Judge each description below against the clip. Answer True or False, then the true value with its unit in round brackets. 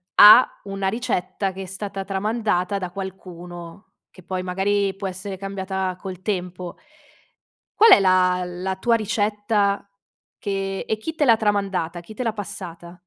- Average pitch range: False (2.0 semitones)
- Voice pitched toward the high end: True (195 Hz)